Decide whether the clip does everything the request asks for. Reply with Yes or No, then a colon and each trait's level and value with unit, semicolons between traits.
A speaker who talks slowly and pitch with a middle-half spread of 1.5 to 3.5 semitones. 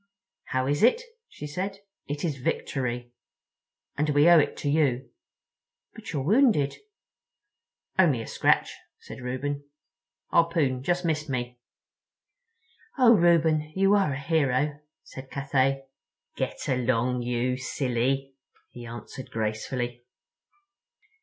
No: slow, 115 wpm; average, 3.9 semitones